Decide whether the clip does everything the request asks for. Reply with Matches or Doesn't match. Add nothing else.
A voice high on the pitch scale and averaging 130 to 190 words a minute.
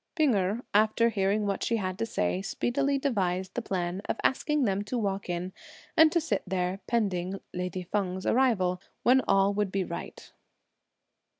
Matches